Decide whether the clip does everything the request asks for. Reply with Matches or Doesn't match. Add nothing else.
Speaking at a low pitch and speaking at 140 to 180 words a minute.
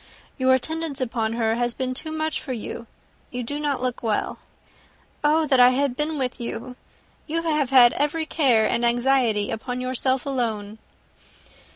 Doesn't match